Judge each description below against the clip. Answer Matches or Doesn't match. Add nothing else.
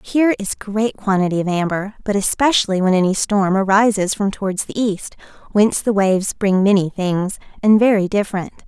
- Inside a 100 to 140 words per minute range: Doesn't match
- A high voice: Matches